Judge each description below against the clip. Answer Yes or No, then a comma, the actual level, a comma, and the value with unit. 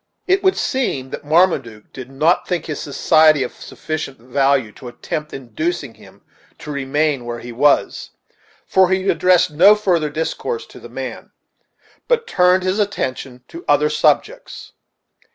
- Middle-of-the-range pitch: Yes, medium, 155 Hz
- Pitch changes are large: Yes, wide, 5.8 semitones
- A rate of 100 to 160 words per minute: Yes, average, 150 wpm